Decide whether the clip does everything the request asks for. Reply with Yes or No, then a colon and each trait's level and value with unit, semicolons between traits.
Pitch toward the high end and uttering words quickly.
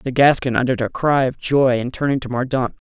No: low, 130 Hz; fast, 230 wpm